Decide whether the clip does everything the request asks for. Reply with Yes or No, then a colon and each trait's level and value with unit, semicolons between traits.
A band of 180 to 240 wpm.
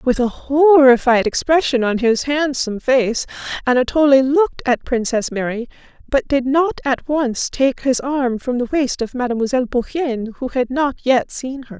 No: average, 170 wpm